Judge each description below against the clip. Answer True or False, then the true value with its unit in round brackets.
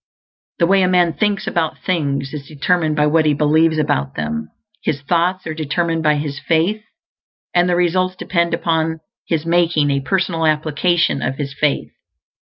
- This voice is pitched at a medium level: True (160 Hz)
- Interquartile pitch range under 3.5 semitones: True (2.9 semitones)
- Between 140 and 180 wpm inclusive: True (170 wpm)